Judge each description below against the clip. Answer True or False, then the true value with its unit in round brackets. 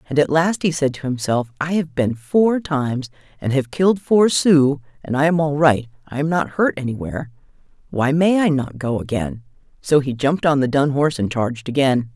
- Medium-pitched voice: True (145 Hz)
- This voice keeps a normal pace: False (210 wpm)